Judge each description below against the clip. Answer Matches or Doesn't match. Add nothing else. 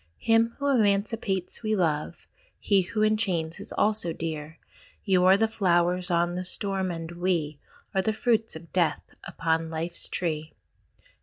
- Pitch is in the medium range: Matches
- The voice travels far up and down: Doesn't match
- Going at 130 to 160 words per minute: Matches